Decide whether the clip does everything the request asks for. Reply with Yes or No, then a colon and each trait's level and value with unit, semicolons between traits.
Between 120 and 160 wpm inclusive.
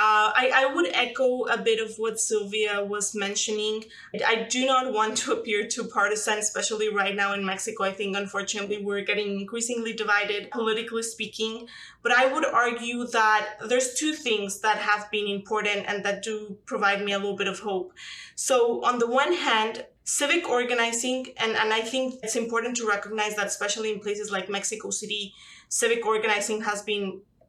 No: average, 180 wpm